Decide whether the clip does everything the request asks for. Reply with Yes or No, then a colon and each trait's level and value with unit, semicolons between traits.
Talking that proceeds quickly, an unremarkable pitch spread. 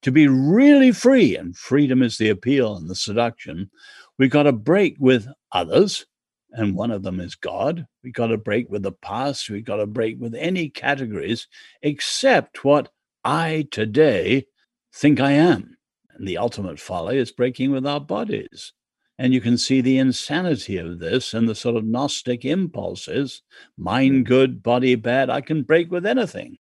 No: average, 175 wpm; average, 4.3 semitones